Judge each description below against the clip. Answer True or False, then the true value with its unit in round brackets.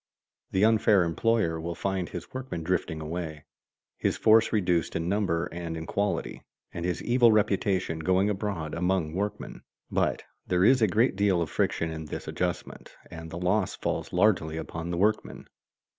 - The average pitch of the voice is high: False (90 Hz)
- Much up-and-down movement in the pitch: False (4.0 semitones)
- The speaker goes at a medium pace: True (160 wpm)